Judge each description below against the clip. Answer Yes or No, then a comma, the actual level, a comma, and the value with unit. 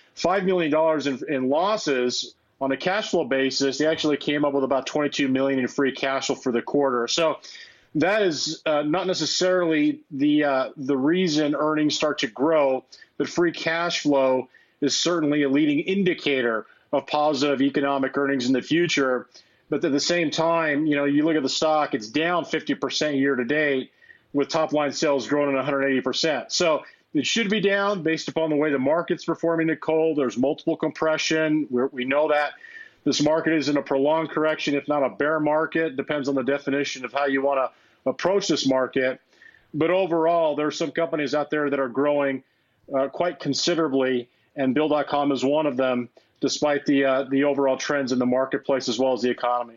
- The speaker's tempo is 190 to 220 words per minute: Yes, average, 200 wpm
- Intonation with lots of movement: No, average, 2.7 semitones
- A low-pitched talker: No, medium, 145 Hz